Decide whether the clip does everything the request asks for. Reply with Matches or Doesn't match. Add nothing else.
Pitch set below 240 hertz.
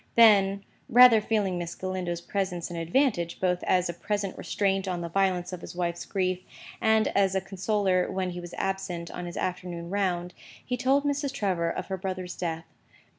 Matches